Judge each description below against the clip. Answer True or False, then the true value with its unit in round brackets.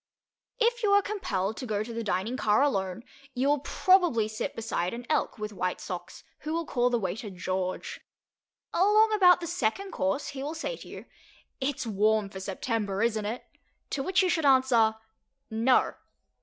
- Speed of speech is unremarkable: True (180 wpm)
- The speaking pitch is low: False (235 Hz)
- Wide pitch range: True (7.4 semitones)